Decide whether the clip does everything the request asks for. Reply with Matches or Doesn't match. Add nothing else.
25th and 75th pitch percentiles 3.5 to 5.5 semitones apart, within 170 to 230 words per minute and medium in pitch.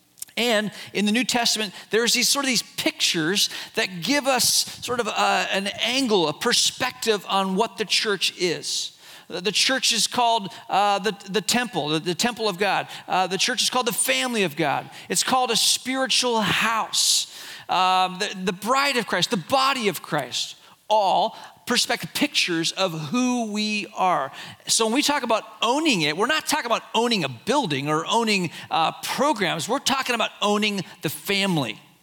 Doesn't match